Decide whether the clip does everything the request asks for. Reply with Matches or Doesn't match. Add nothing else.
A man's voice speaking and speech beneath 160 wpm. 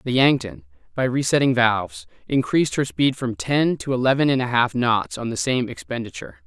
Doesn't match